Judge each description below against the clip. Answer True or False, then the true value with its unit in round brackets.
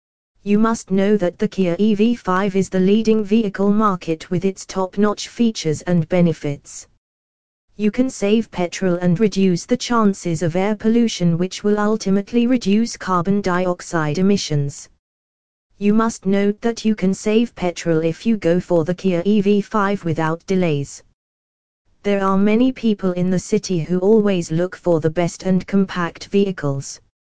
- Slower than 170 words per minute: True (155 wpm)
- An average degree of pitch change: True (3.9 semitones)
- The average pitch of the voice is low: False (190 Hz)